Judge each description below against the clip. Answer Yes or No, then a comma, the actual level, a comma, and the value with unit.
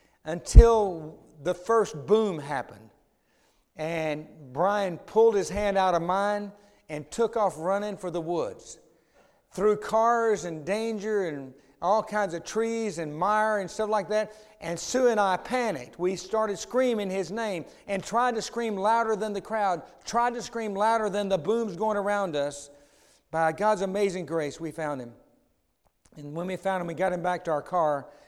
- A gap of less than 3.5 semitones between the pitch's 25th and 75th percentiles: No, average, 4.7 semitones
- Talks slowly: No, average, 175 wpm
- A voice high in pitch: Yes, high, 200 Hz